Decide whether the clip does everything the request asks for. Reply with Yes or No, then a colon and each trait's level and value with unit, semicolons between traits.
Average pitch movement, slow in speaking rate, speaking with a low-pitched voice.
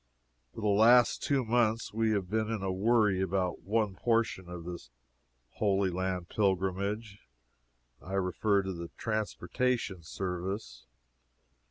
Yes: average, 3.1 semitones; slow, 125 wpm; low, 100 Hz